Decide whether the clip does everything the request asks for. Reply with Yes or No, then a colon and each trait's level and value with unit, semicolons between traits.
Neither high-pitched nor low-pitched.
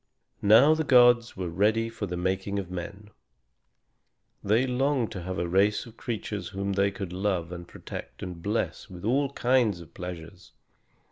No: low, 100 Hz